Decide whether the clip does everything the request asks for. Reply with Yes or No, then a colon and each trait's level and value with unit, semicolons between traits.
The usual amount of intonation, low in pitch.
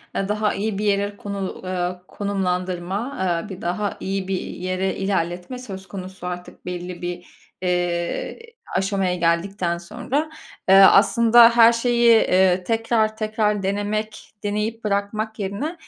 No: average, 3.0 semitones; high, 195 Hz